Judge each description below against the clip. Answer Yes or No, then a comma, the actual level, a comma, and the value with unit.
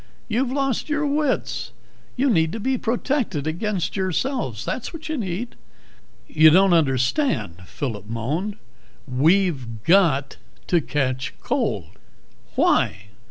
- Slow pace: Yes, slow, 115 wpm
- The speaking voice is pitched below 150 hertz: No, medium, 180 Hz